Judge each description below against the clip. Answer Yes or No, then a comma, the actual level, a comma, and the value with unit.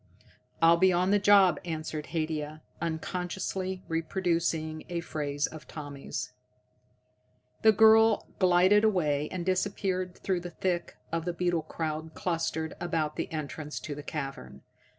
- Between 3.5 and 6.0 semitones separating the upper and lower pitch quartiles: No, average, 3.0 semitones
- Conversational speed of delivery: No, slow, 130 wpm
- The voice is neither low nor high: Yes, medium, 170 Hz